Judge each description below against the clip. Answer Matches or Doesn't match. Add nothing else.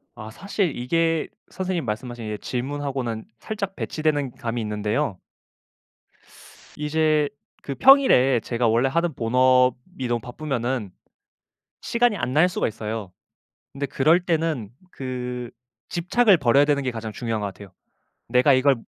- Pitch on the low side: Matches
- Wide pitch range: Doesn't match